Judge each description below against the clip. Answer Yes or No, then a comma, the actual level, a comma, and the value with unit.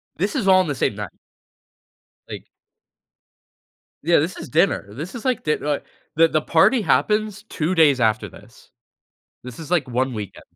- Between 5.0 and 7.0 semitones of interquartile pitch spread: Yes, average, 5.3 semitones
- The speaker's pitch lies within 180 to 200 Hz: No, medium, 165 Hz